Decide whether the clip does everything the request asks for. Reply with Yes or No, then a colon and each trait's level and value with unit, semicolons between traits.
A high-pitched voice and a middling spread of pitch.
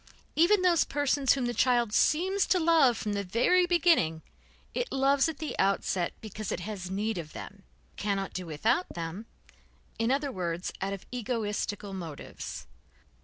No: high, 225 Hz; wide, 7.2 semitones